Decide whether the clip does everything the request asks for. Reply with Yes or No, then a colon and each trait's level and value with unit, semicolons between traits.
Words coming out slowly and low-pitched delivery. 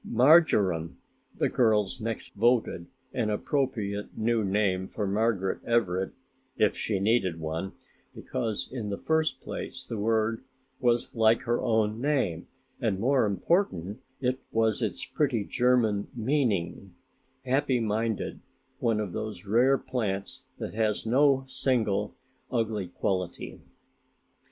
Yes: slow, 120 wpm; low, 110 Hz